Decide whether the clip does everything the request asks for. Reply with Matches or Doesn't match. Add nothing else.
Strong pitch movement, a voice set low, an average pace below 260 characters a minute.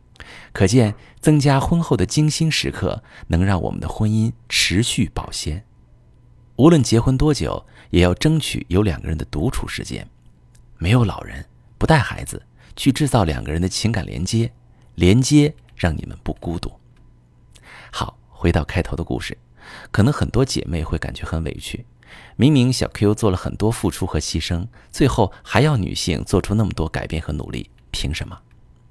Matches